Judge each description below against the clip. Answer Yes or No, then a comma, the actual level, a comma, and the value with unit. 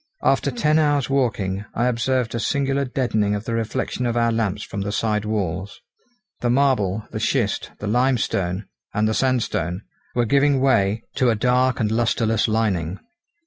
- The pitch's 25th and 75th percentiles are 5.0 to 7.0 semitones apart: No, average, 3.7 semitones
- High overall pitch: No, low, 115 Hz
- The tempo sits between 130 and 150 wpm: No, average, 165 wpm